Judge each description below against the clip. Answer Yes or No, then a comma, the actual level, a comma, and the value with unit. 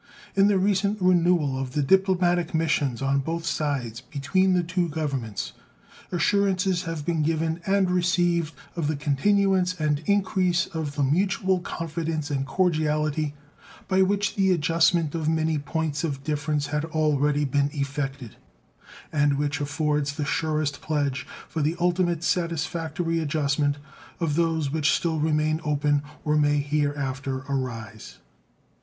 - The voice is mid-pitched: Yes, medium, 155 Hz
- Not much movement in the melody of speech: No, average, 3.3 semitones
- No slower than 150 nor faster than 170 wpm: No, slow, 135 wpm